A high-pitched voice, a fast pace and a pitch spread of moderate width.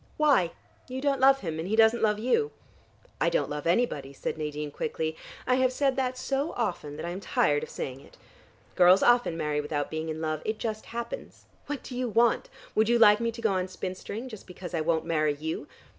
No: high, 205 Hz; fast, 220 wpm; wide, 7.5 semitones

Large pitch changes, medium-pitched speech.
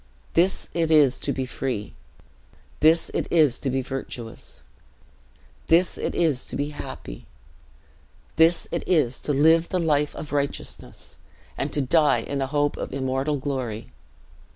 No: average, 3.4 semitones; medium, 145 Hz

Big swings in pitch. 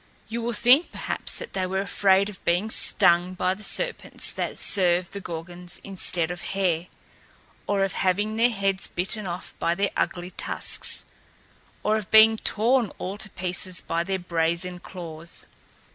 No: average, 3.0 semitones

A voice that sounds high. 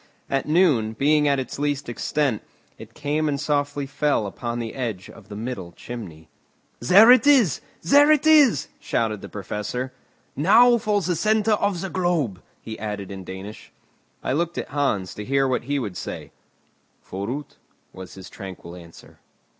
No: low, 135 Hz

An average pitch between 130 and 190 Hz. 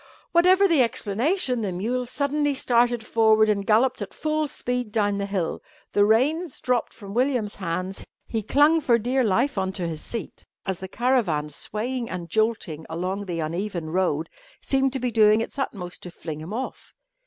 No: high, 220 Hz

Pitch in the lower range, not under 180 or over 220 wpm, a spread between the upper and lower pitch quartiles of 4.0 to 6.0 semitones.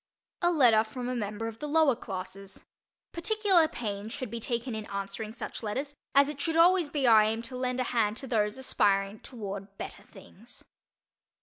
No: high, 235 Hz; average, 185 wpm; average, 4.9 semitones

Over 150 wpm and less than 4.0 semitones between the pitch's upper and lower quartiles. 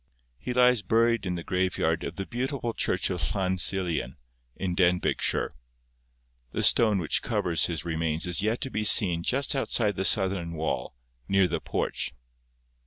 No: average, 160 wpm; average, 4.5 semitones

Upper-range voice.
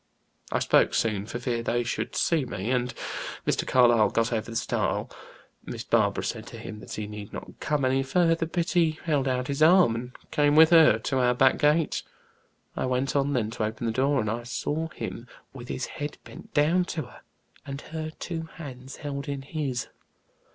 No: low, 135 Hz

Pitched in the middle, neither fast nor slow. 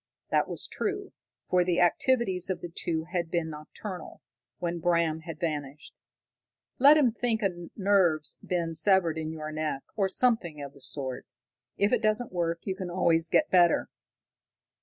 Yes: medium, 175 Hz; average, 160 wpm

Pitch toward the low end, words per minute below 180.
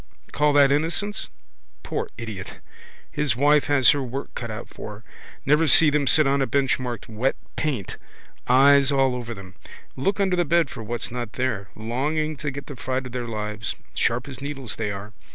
No: low, 130 Hz; average, 190 wpm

